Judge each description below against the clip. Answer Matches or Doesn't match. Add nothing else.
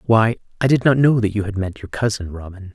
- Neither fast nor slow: Doesn't match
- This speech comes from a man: Matches